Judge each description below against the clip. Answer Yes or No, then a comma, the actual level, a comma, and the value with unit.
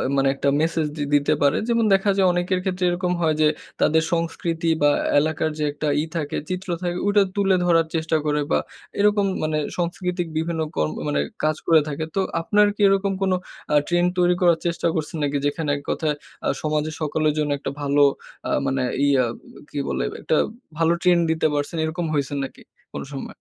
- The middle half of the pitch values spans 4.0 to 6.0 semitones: No, average, 3.0 semitones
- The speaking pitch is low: No, medium, 160 Hz